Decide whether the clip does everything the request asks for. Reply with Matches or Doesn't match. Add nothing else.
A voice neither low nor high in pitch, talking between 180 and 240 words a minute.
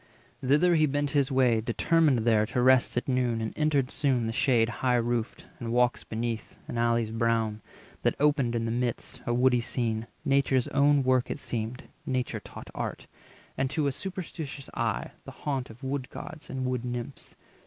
Doesn't match